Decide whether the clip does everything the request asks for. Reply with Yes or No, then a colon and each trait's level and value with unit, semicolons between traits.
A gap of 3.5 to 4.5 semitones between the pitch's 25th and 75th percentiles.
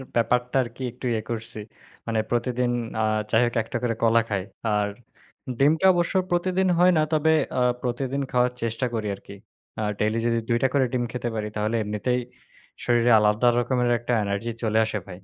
No: narrow, 2.5 semitones